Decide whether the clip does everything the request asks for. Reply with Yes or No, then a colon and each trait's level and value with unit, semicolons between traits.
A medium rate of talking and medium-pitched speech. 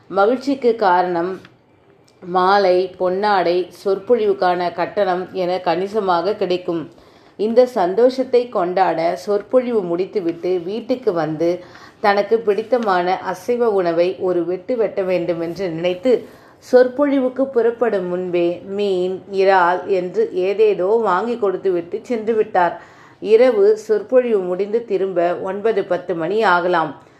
No: average, 100 wpm; high, 195 Hz